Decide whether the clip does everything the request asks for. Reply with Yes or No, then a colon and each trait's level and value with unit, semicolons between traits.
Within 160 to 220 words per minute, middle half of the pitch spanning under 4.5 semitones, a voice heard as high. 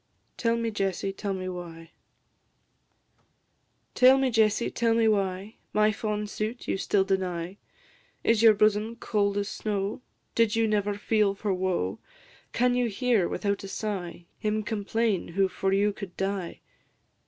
No: average, 150 wpm; narrow, 2.4 semitones; high, 205 Hz